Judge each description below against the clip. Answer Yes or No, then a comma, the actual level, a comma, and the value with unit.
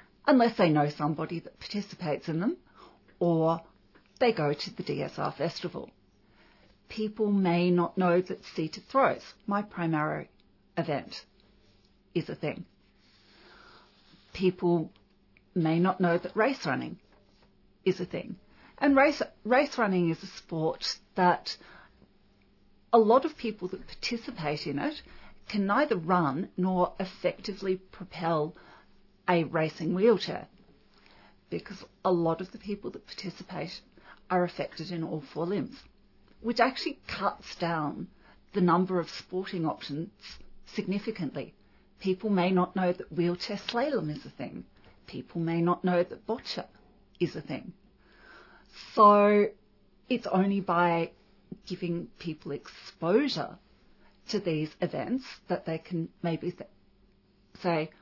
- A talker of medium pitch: Yes, medium, 180 Hz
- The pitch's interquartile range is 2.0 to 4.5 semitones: Yes, average, 3.8 semitones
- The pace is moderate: No, slow, 125 wpm